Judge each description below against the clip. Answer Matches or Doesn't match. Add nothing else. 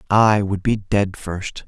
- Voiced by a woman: Doesn't match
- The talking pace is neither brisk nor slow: Matches